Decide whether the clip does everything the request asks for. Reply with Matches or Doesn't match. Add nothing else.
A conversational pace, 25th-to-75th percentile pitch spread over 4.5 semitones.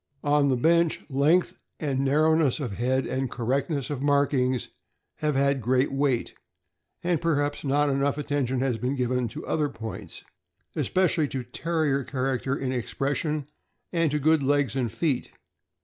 Doesn't match